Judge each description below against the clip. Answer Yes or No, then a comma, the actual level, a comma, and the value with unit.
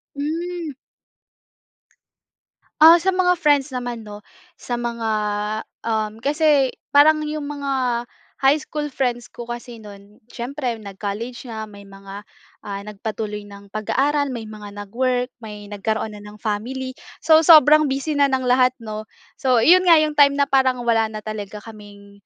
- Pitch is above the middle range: Yes, high, 245 Hz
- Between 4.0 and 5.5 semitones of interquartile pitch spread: Yes, average, 5.1 semitones